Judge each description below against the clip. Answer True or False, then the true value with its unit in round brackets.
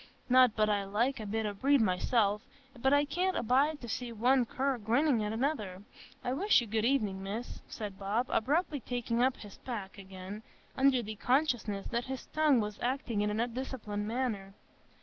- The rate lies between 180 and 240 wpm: True (185 wpm)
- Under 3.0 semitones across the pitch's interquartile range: False (4.1 semitones)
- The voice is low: False (235 Hz)